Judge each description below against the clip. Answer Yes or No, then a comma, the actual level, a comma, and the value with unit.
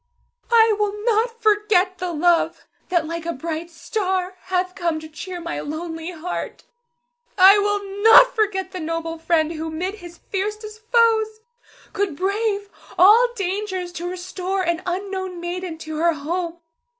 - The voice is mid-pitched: No, very high, 370 Hz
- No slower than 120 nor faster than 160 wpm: Yes, average, 150 wpm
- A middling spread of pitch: Yes, average, 3.5 semitones